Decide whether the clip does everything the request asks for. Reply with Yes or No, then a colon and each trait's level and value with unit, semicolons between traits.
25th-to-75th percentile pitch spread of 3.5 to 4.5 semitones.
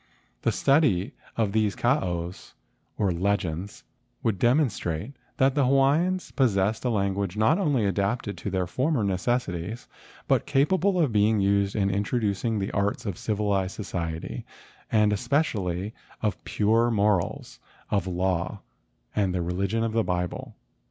Yes: average, 4.1 semitones